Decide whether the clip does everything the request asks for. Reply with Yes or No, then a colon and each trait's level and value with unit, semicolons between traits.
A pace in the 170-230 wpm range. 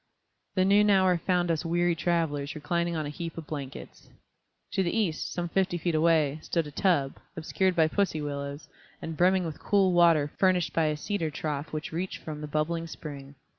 Yes: average, 190 wpm